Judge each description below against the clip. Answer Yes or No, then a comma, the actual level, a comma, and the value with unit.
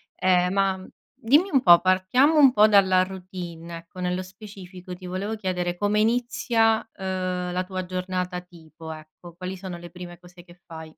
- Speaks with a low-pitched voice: No, medium, 185 Hz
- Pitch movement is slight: Yes, narrow, 2.0 semitones